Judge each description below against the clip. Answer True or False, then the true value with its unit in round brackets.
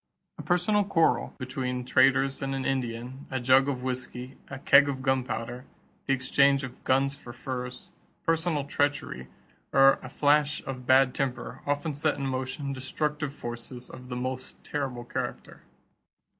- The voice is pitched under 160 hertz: True (135 Hz)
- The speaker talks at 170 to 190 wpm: False (150 wpm)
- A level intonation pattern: True (1.9 semitones)